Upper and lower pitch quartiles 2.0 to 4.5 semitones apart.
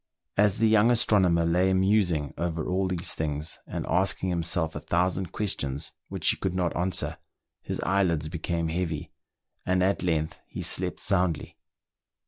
Yes: narrow, 2.6 semitones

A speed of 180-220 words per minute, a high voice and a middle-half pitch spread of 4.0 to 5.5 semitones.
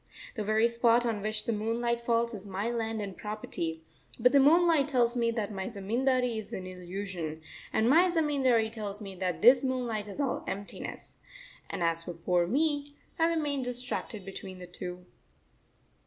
No: average, 170 wpm; high, 225 Hz; average, 4.4 semitones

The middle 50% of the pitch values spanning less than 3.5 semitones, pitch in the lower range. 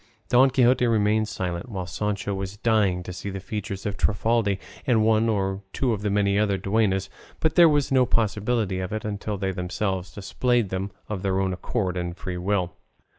Yes: average, 2.7 semitones; low, 100 Hz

